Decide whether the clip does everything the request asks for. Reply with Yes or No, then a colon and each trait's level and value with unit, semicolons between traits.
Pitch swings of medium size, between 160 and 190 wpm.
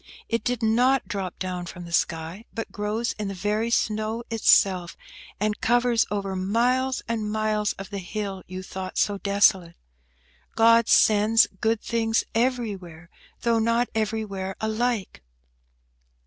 No: average, 3.1 semitones; slow, 135 wpm